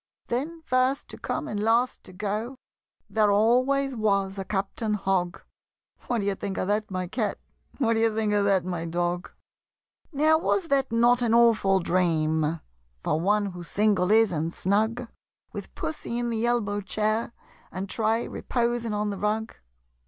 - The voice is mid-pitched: No, high, 210 Hz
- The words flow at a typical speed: Yes, average, 160 wpm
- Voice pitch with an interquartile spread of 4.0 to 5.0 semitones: No, average, 3.5 semitones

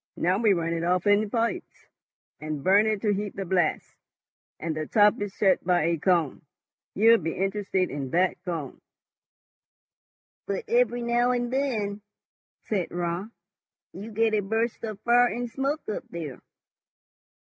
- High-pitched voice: Yes, high, 200 Hz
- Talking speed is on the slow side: No, average, 155 wpm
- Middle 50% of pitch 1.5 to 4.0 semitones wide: No, average, 4.5 semitones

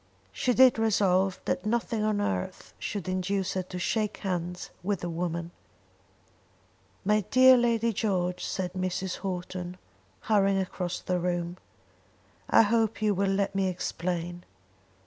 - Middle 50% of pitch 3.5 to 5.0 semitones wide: No, average, 2.9 semitones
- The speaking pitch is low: No, high, 190 Hz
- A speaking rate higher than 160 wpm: No, slow, 135 wpm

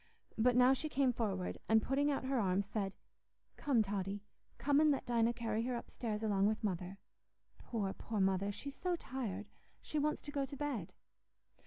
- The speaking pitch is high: Yes, high, 230 Hz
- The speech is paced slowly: No, average, 175 wpm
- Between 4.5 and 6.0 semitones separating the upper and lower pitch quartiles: Yes, average, 5.2 semitones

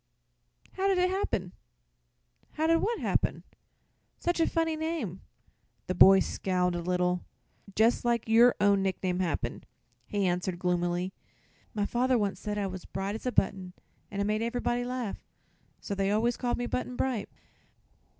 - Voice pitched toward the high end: Yes, high, 205 Hz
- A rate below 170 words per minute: Yes, average, 160 wpm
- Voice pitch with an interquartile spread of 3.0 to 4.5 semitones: No, average, 5.0 semitones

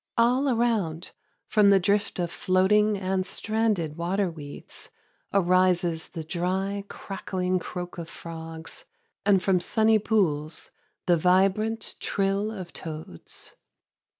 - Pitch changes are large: No, average, 3.3 semitones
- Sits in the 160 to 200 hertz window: Yes, medium, 185 Hz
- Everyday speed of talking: No, slow, 115 wpm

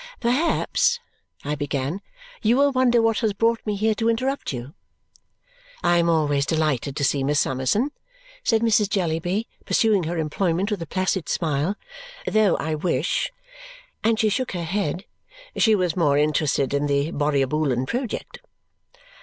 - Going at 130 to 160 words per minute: Yes, average, 150 wpm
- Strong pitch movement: Yes, wide, 7.0 semitones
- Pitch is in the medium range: Yes, medium, 175 Hz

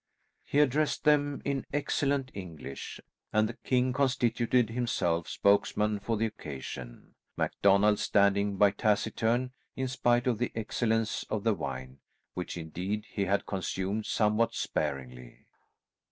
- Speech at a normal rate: No, slow, 125 wpm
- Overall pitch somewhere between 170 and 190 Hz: No, low, 105 Hz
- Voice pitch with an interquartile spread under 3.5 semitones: No, average, 4.3 semitones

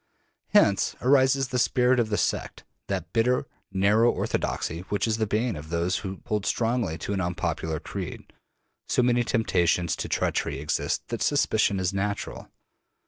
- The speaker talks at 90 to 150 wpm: No, average, 160 wpm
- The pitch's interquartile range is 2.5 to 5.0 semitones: No, wide, 5.4 semitones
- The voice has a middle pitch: No, low, 100 Hz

